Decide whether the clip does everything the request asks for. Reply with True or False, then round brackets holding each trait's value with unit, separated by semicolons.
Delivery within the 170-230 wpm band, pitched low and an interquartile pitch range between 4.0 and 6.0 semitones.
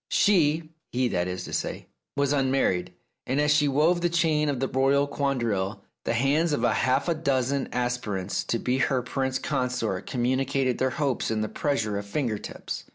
False (190 wpm; 130 Hz; 3.3 semitones)